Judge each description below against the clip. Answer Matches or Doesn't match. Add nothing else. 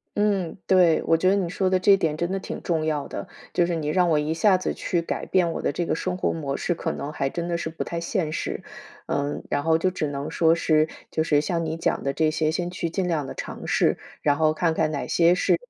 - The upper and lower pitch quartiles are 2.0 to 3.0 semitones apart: Matches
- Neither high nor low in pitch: Matches